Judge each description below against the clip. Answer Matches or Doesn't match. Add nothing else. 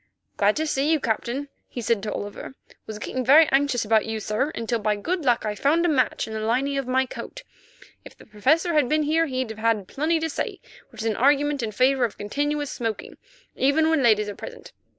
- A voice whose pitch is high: Matches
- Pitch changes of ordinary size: Matches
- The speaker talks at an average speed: Doesn't match